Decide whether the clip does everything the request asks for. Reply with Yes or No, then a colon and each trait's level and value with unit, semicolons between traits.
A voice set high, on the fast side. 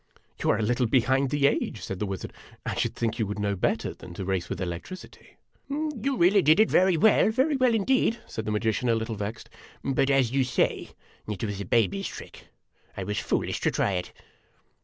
No: low, 115 Hz; fast, 225 wpm